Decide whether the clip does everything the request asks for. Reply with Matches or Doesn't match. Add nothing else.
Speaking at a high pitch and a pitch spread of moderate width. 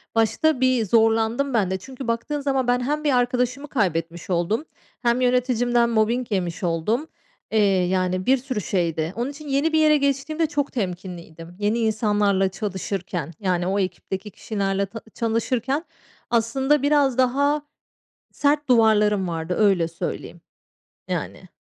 Doesn't match